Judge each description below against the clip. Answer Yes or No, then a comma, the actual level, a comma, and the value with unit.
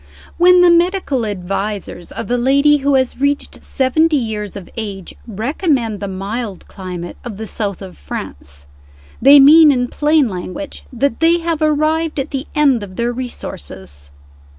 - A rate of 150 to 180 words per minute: Yes, average, 155 wpm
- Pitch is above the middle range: Yes, high, 245 Hz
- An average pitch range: No, wide, 6.8 semitones